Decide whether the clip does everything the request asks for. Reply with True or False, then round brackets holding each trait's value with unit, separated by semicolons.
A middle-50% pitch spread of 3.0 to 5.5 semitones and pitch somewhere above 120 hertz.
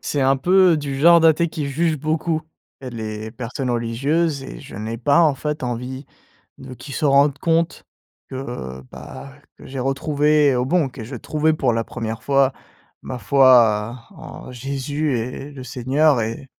True (3.7 semitones; 135 Hz)